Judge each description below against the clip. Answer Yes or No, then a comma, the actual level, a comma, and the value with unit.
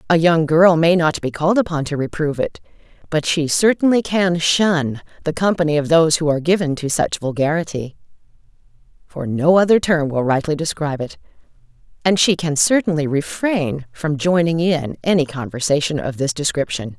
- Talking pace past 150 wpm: Yes, average, 165 wpm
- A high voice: No, medium, 160 Hz